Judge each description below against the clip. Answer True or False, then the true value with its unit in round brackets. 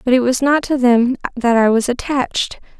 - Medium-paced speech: False (215 wpm)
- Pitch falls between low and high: False (250 Hz)